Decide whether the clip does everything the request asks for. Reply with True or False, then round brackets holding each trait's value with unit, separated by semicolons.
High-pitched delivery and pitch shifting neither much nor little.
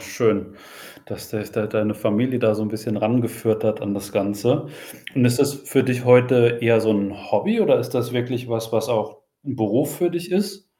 False (115 Hz; 3.0 semitones)